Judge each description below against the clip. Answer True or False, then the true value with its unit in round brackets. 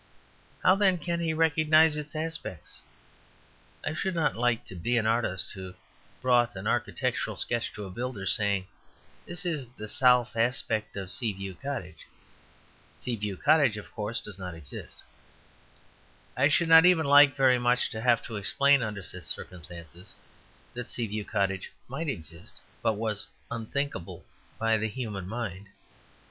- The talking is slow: False (155 wpm)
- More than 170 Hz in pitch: False (115 Hz)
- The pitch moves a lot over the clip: True (6.2 semitones)